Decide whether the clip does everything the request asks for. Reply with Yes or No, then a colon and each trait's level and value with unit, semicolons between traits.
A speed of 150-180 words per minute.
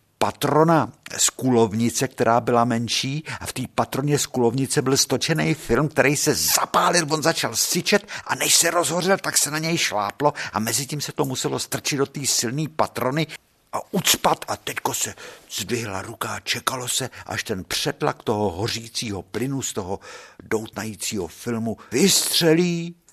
Yes: average, 160 wpm